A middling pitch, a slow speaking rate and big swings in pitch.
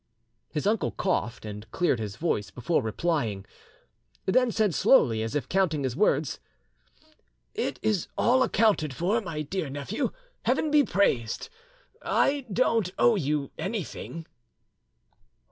Yes: medium, 165 Hz; slow, 130 wpm; wide, 8.3 semitones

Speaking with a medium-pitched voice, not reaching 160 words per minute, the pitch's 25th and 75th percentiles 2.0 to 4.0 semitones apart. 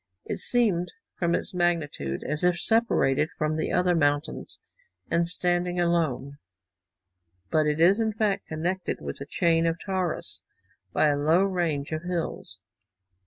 Yes: medium, 170 Hz; average, 145 wpm; average, 2.8 semitones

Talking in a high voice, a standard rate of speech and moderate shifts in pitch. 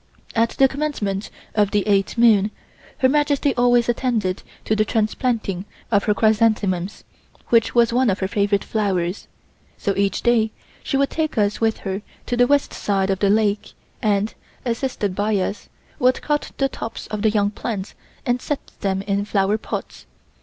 Yes: high, 215 Hz; average, 170 wpm; average, 3.3 semitones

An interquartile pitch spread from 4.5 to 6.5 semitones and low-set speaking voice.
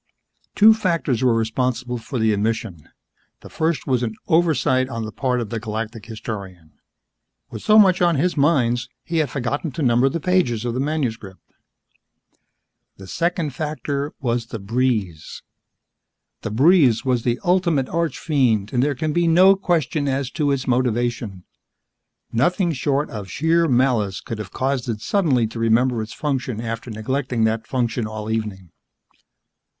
Yes: average, 5.0 semitones; low, 125 Hz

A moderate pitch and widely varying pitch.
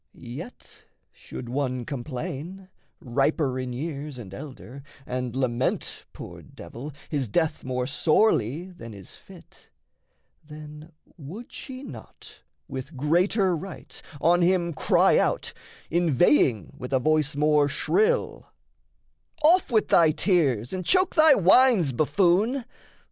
Yes: medium, 150 Hz; wide, 5.9 semitones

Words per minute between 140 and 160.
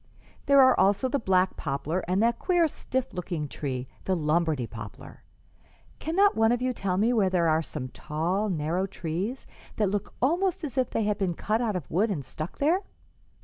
No: average, 190 wpm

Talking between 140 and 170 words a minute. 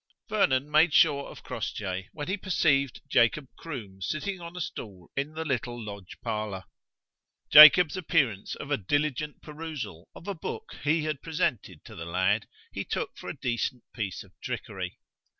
Yes: average, 165 wpm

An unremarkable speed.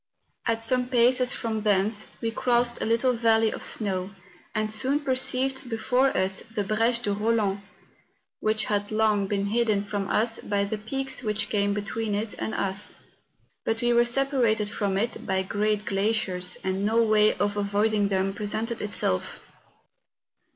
Yes: average, 160 wpm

